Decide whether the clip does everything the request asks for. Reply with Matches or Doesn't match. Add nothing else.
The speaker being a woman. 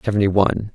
Doesn't match